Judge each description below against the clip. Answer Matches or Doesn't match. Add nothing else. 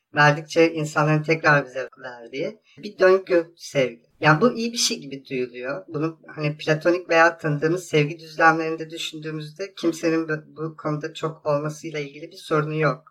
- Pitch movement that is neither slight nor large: Doesn't match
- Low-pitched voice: Doesn't match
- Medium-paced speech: Doesn't match